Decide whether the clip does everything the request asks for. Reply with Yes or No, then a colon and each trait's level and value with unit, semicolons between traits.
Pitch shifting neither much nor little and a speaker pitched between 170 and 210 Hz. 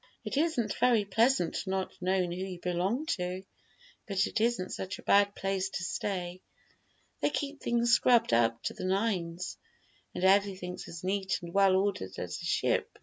Yes: average, 3.0 semitones; high, 190 Hz